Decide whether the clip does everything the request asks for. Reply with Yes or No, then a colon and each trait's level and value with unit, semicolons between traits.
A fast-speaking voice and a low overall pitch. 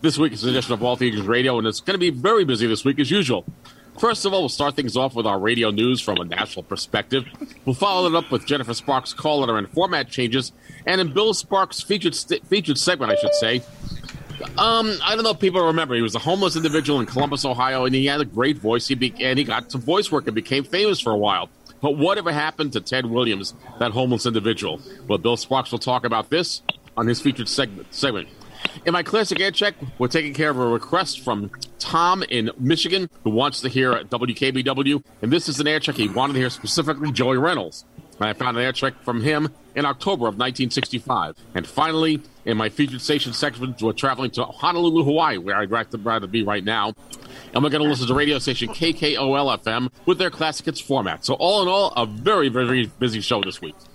Yes: fast, 225 wpm; low, 130 Hz